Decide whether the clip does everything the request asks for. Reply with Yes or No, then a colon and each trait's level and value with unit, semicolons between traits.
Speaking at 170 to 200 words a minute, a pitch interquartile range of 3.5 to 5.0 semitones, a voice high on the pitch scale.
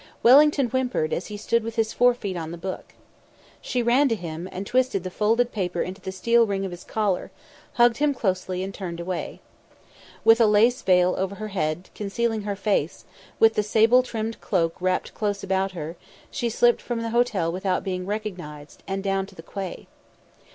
Yes: average, 195 wpm; average, 4.0 semitones; high, 200 Hz